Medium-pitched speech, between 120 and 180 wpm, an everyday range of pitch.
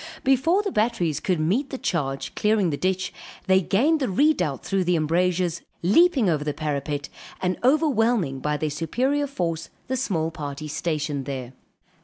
No: medium, 180 Hz; average, 160 wpm; wide, 8.2 semitones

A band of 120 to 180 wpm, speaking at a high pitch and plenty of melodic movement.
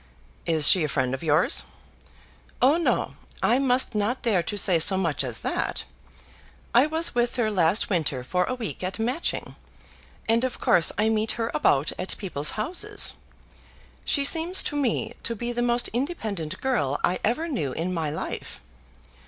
Yes: average, 170 wpm; high, 215 Hz; wide, 7.2 semitones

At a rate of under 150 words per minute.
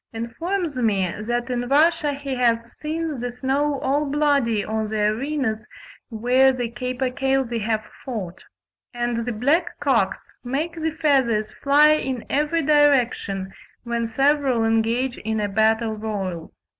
Yes: average, 140 wpm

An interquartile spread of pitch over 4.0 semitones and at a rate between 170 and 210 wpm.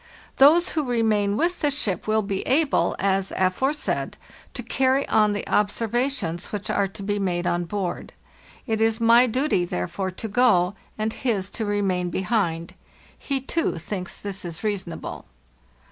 No: average, 4.8 semitones; average, 150 wpm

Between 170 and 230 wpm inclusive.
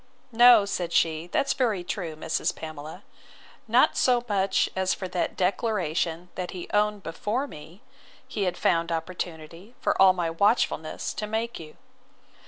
No: average, 150 wpm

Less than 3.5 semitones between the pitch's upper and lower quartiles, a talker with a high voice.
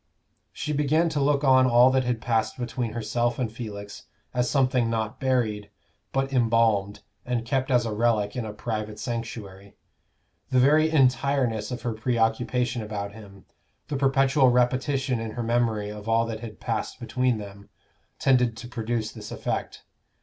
No: average, 2.9 semitones; low, 120 Hz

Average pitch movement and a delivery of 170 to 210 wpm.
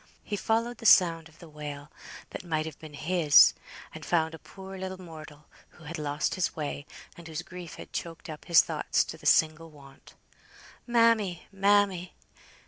Yes: average, 3.5 semitones; average, 175 wpm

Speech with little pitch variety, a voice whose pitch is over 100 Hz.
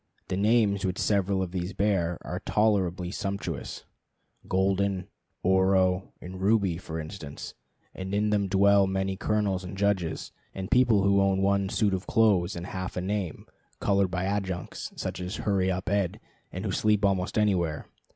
No: narrow, 1.6 semitones; very low, 95 Hz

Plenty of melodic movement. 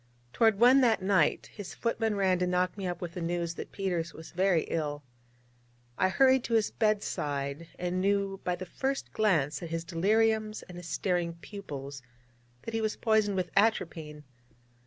No: average, 4.2 semitones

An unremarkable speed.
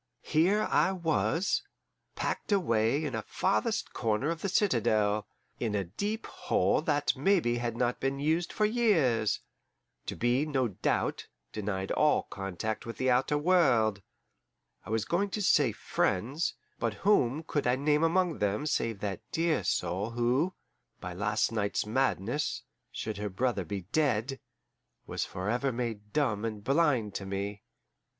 Yes: average, 150 wpm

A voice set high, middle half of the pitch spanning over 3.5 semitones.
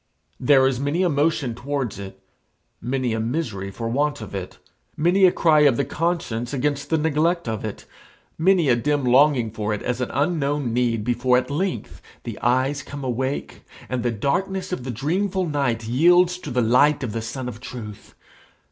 No: low, 135 Hz; average, 4.1 semitones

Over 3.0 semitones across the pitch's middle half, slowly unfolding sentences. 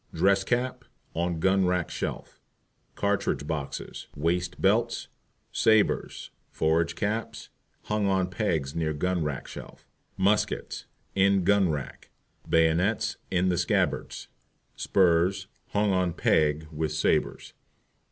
Yes: average, 3.5 semitones; slow, 115 wpm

